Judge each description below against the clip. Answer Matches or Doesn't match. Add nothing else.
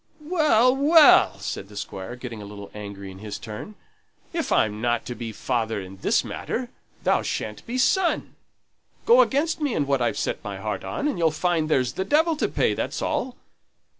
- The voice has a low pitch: Doesn't match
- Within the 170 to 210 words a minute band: Matches